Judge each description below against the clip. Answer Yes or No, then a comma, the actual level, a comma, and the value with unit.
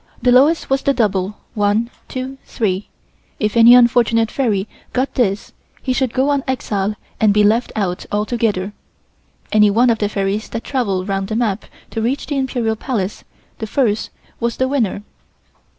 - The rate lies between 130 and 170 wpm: Yes, average, 165 wpm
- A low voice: No, high, 225 Hz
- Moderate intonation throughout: Yes, average, 3.6 semitones